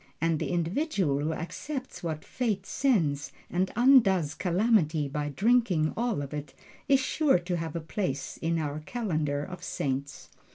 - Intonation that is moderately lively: No, wide, 6.8 semitones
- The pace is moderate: Yes, average, 155 wpm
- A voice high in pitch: No, medium, 170 Hz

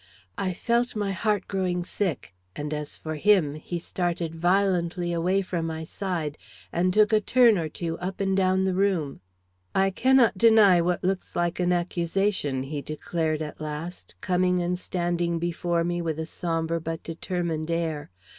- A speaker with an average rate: Yes, average, 165 wpm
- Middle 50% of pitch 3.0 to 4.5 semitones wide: No, narrow, 2.6 semitones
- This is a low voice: No, medium, 175 Hz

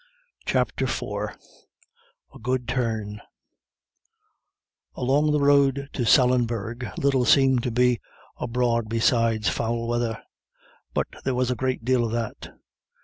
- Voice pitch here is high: No, low, 120 Hz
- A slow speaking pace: Yes, slow, 120 wpm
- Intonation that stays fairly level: Yes, narrow, 2.0 semitones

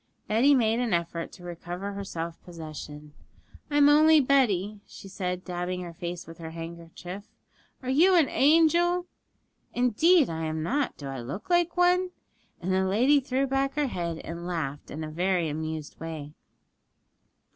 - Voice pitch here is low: No, medium, 185 Hz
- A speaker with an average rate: Yes, average, 160 wpm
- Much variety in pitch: Yes, wide, 8.7 semitones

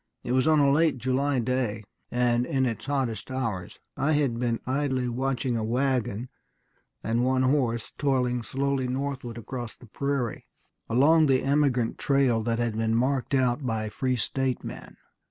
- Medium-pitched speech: No, low, 130 Hz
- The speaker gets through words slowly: No, average, 160 wpm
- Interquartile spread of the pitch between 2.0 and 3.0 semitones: Yes, narrow, 2.6 semitones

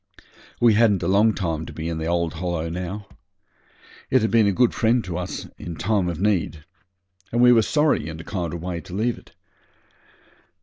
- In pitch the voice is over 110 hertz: No, very low, 90 Hz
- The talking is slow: No, fast, 205 wpm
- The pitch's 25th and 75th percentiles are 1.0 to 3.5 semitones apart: No, average, 4.7 semitones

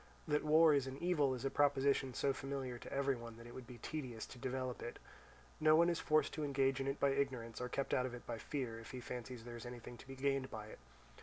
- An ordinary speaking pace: No, fast, 260 wpm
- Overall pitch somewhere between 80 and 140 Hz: Yes, low, 135 Hz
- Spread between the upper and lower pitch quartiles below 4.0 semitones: Yes, narrow, 2.5 semitones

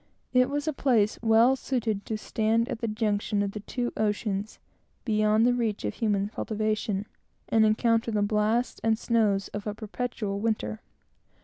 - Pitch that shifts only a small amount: Yes, narrow, 1.9 semitones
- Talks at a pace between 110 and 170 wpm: Yes, average, 165 wpm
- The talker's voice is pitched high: Yes, high, 215 Hz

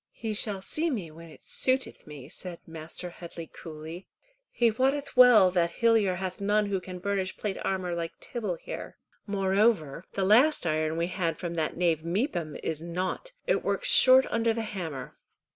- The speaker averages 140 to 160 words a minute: No, average, 175 wpm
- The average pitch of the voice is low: No, medium, 185 Hz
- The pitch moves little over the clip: No, average, 4.7 semitones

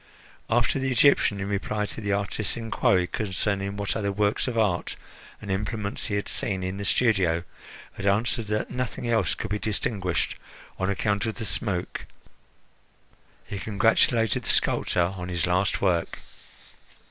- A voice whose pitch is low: Yes, low, 100 Hz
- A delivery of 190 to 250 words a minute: No, average, 155 wpm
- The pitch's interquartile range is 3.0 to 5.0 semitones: No, narrow, 2.6 semitones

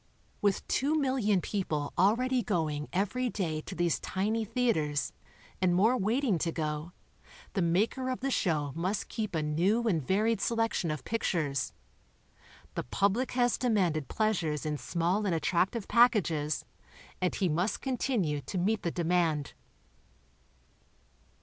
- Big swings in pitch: Yes, wide, 5.8 semitones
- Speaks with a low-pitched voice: No, high, 190 Hz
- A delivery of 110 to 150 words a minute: Yes, average, 140 wpm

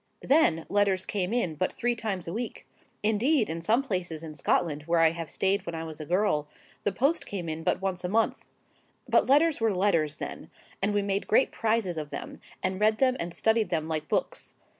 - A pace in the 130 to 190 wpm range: No, fast, 205 wpm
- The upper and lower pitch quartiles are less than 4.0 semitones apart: No, average, 5.0 semitones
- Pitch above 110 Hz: Yes, high, 190 Hz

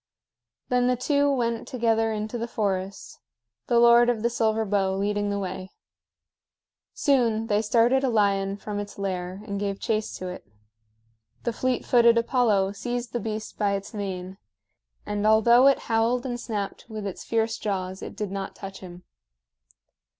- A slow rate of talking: No, average, 165 wpm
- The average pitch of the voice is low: No, high, 215 Hz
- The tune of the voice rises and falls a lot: No, average, 3.0 semitones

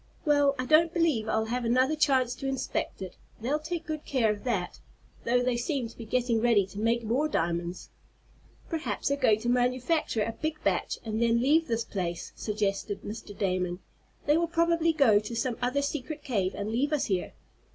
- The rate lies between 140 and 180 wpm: No, average, 195 wpm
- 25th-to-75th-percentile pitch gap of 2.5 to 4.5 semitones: No, average, 5.1 semitones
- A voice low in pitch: No, high, 245 Hz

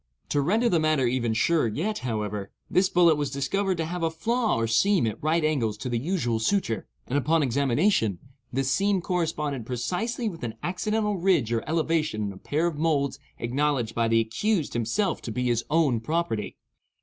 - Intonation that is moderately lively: No, wide, 6.9 semitones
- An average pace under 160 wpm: No, average, 185 wpm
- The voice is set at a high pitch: No, medium, 150 Hz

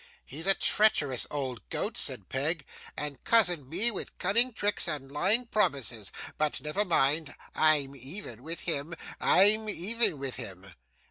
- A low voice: No, medium, 155 Hz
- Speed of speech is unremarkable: Yes, average, 145 wpm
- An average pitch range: No, wide, 6.8 semitones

